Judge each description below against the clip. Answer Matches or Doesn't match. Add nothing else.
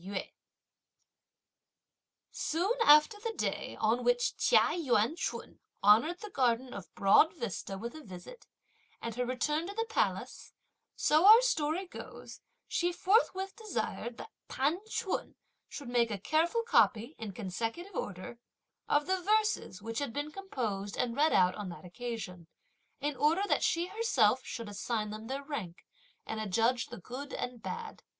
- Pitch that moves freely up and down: Matches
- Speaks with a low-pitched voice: Doesn't match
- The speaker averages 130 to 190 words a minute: Matches